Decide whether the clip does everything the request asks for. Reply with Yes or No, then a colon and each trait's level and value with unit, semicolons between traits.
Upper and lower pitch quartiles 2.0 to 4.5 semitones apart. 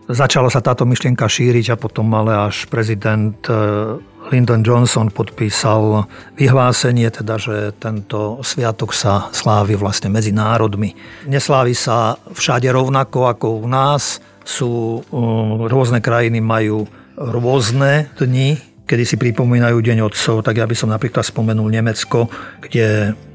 Yes: narrow, 2.4 semitones